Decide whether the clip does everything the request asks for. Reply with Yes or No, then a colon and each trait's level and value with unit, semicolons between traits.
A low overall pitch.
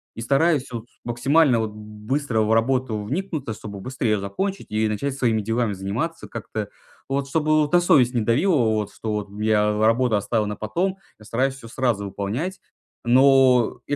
Yes: low, 120 Hz